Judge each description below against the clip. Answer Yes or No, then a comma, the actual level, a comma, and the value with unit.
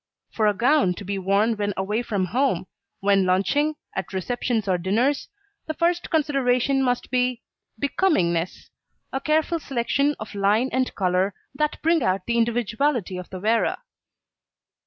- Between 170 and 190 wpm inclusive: No, average, 150 wpm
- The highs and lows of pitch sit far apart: Yes, wide, 5.9 semitones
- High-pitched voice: Yes, high, 230 Hz